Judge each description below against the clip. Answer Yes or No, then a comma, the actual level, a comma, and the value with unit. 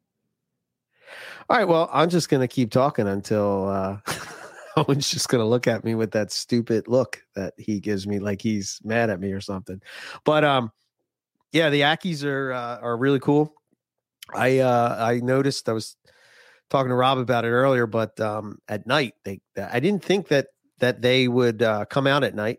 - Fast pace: No, average, 185 wpm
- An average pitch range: Yes, average, 4.6 semitones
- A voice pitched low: Yes, low, 120 Hz